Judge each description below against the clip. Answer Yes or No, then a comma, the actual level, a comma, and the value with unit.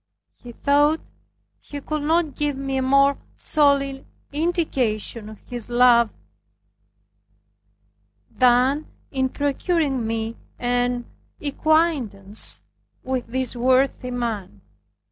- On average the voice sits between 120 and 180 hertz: No, very high, 260 Hz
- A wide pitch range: No, average, 3.2 semitones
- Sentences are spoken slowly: Yes, slow, 95 wpm